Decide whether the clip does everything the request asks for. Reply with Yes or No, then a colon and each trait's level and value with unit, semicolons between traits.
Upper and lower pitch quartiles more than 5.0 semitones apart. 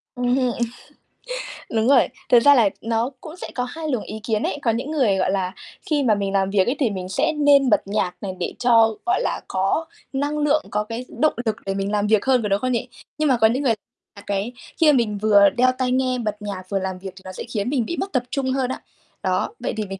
No: average, 4.6 semitones